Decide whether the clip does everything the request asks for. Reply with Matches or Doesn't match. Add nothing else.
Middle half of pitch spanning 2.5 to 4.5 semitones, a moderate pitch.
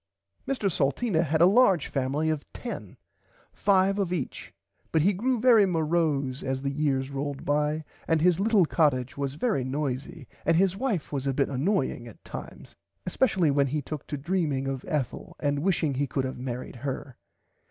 Doesn't match